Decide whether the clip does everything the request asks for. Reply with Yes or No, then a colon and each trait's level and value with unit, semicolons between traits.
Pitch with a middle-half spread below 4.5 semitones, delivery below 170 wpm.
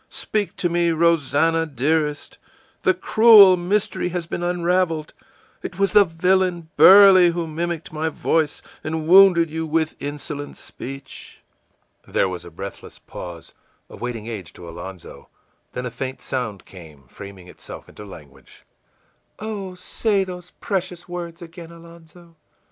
No: average, 5.2 semitones; slow, 135 wpm